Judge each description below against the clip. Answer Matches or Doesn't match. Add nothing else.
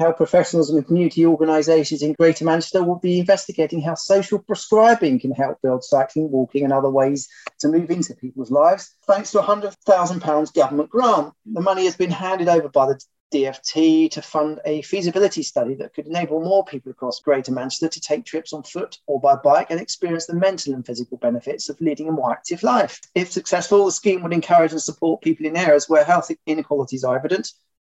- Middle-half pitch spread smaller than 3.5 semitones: Doesn't match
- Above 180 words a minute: Matches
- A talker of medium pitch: Matches